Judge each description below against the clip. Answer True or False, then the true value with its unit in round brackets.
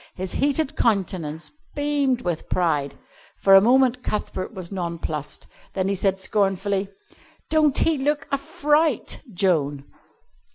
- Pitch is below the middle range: False (195 Hz)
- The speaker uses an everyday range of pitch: False (7.3 semitones)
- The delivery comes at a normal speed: False (125 wpm)